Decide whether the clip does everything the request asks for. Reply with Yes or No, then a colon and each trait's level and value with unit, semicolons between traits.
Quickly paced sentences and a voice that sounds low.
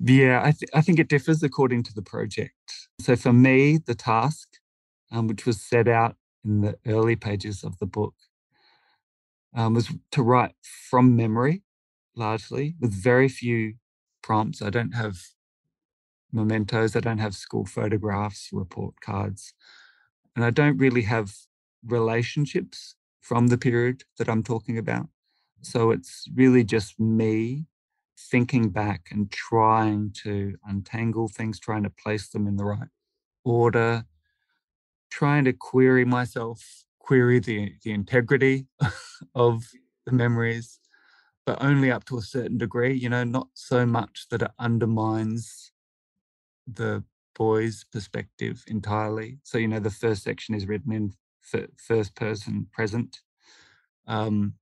No: average, 140 wpm; low, 115 Hz